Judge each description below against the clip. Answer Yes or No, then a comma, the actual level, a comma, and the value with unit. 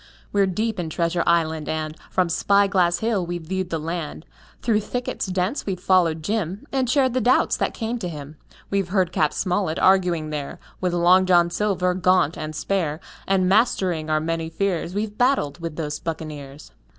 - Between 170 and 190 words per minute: Yes, average, 180 wpm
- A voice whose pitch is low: No, medium, 180 Hz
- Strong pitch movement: No, average, 3.6 semitones